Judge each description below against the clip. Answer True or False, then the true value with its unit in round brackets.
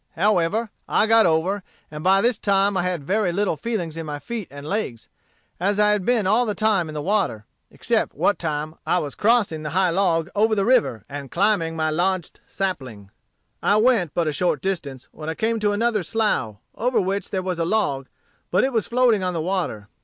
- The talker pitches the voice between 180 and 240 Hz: True (190 Hz)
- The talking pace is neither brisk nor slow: False (210 wpm)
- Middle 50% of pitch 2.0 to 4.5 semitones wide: False (4.9 semitones)